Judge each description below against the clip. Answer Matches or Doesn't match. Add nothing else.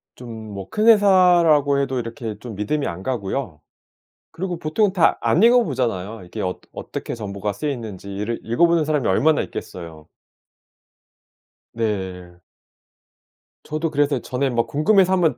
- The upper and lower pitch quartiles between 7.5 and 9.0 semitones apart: Matches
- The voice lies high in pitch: Doesn't match